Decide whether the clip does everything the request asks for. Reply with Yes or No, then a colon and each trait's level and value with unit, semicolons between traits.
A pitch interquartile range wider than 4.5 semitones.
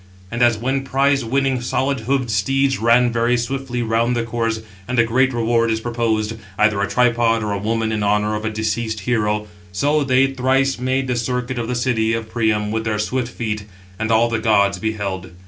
No: narrow, 2.5 semitones